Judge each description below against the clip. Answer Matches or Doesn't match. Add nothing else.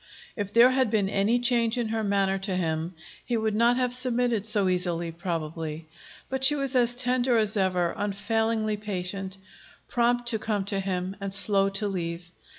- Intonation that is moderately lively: Matches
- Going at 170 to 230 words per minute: Matches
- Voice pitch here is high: Matches